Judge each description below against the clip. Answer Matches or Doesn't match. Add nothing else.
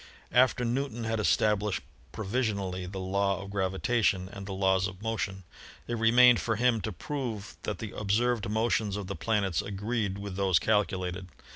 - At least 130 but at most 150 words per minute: Doesn't match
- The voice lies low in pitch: Matches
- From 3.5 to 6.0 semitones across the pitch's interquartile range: Doesn't match